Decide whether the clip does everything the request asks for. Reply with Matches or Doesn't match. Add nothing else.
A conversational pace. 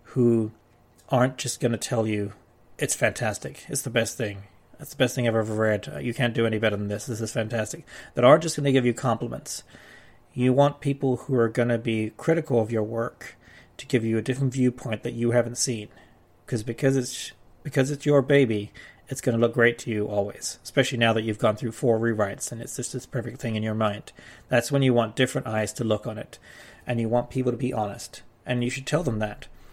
Doesn't match